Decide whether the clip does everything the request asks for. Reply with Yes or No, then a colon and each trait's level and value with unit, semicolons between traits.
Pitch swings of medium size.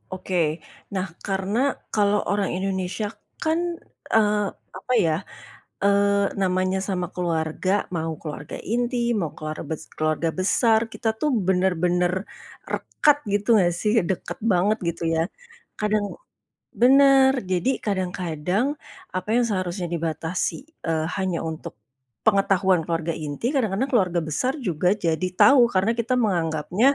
Yes: average, 3.6 semitones